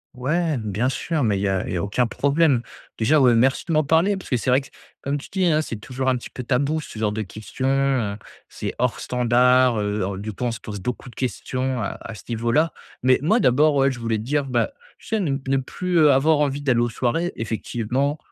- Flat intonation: No, average, 4.1 semitones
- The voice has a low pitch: Yes, low, 130 Hz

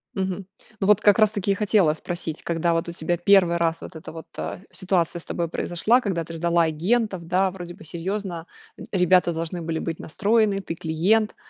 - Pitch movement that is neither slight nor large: Yes, average, 3.0 semitones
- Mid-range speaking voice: Yes, medium, 175 Hz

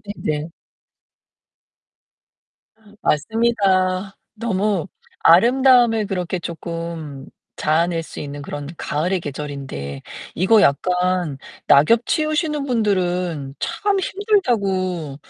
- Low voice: No, medium, 185 Hz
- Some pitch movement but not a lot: No, wide, 6.7 semitones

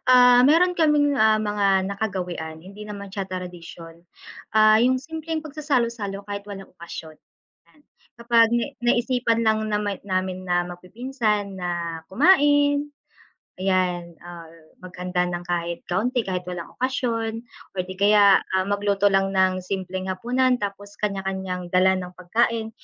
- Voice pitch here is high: Yes, high, 200 Hz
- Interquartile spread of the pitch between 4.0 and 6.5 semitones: Yes, average, 4.4 semitones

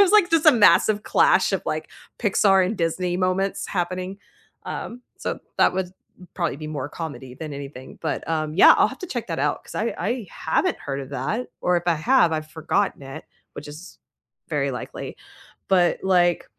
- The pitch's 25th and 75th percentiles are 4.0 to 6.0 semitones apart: Yes, average, 4.8 semitones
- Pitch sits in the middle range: Yes, medium, 180 Hz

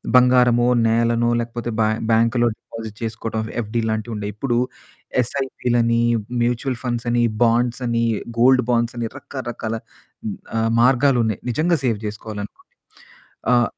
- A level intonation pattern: Yes, narrow, 1.4 semitones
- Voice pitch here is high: No, low, 120 Hz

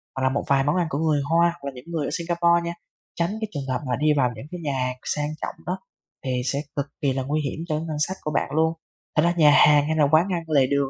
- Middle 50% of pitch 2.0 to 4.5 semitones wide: Yes, average, 3.3 semitones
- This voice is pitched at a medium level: Yes, medium, 150 Hz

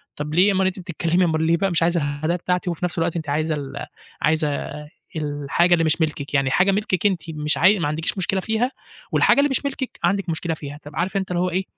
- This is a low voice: No, medium, 170 Hz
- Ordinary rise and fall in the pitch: Yes, average, 3.4 semitones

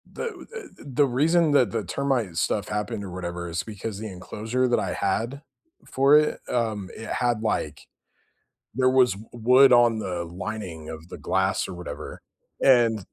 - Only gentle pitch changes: No, average, 5.2 semitones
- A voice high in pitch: No, low, 110 Hz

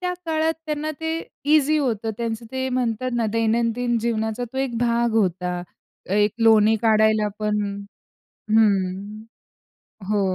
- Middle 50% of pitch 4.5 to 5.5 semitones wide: No, average, 2.9 semitones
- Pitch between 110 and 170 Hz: No, high, 225 Hz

